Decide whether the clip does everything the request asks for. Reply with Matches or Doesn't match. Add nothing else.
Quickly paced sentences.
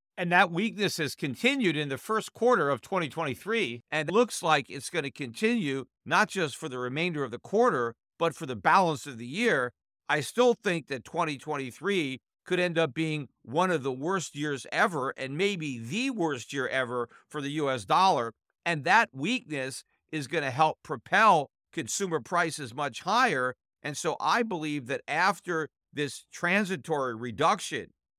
Doesn't match